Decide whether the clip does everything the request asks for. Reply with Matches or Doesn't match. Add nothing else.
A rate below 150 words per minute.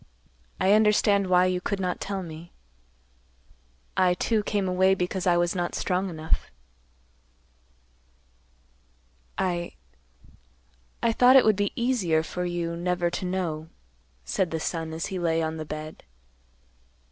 Matches